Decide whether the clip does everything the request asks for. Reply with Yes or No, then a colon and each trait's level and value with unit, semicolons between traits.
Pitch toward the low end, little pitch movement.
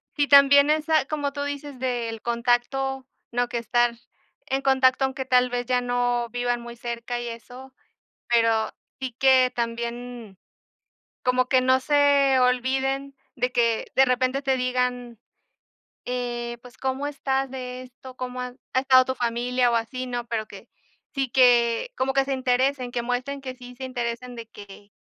No: very high, 250 Hz; narrow, 1.8 semitones